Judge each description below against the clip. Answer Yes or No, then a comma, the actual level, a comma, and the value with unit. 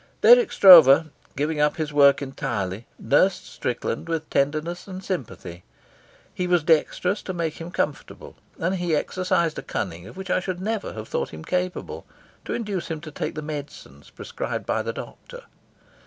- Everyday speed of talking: Yes, average, 170 wpm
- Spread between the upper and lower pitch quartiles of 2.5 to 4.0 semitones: No, average, 4.4 semitones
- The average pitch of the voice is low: No, medium, 160 Hz